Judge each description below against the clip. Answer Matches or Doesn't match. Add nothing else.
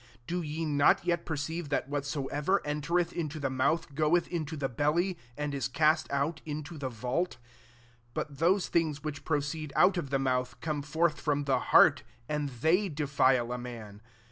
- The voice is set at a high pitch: Doesn't match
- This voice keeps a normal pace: Matches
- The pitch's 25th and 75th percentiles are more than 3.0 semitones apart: Doesn't match